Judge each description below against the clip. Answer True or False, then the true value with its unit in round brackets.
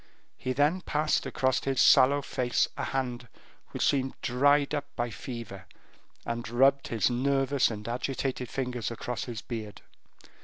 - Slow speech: False (145 wpm)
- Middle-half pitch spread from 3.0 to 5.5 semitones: False (2.5 semitones)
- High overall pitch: False (130 Hz)